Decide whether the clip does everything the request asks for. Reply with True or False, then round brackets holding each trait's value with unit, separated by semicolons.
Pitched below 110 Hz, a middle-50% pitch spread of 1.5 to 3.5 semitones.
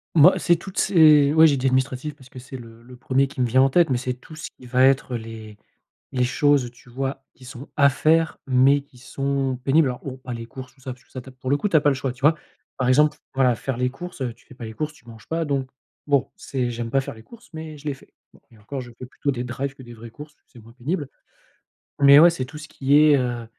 False (135 Hz; 2.6 semitones)